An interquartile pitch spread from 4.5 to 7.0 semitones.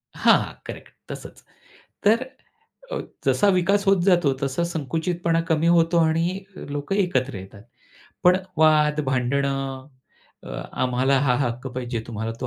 Yes: average, 4.9 semitones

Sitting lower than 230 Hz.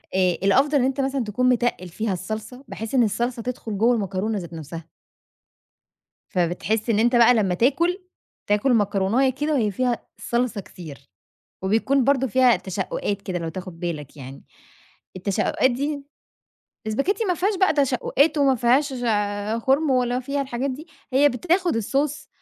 No: high, 240 Hz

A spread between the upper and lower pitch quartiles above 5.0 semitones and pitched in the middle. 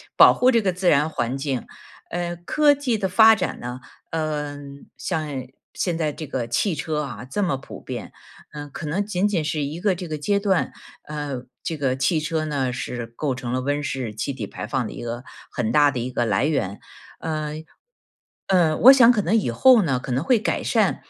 Yes: wide, 5.6 semitones; medium, 150 Hz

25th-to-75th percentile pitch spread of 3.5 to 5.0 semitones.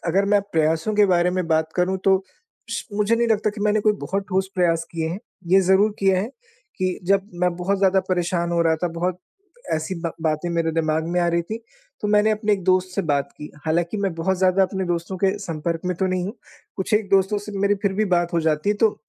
No: average, 2.9 semitones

